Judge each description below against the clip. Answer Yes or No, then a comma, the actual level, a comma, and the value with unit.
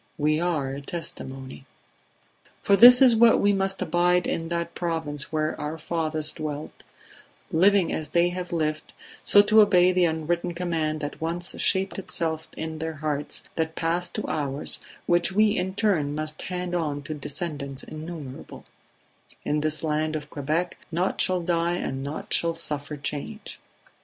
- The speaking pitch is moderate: Yes, medium, 160 Hz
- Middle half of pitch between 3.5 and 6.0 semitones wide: No, average, 2.8 semitones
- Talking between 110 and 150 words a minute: No, average, 160 wpm